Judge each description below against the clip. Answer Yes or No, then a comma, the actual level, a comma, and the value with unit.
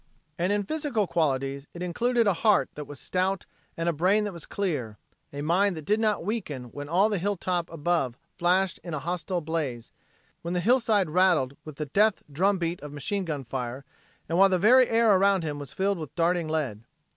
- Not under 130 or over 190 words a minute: No, fast, 205 wpm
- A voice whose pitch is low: No, medium, 175 Hz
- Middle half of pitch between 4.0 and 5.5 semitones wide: Yes, average, 5.2 semitones